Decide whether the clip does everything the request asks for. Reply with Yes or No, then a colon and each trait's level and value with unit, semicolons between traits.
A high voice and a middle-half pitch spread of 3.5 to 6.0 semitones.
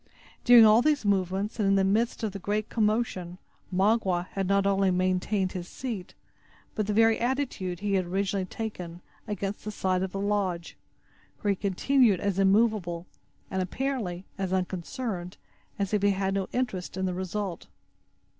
No: high, 195 Hz; narrow, 2.5 semitones